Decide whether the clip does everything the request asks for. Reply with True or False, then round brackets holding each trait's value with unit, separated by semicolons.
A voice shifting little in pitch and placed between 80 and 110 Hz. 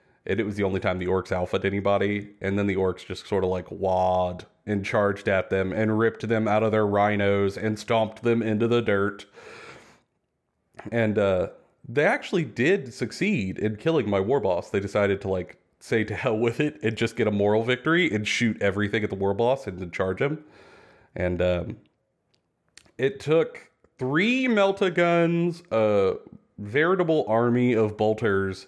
False (3.2 semitones; 105 Hz)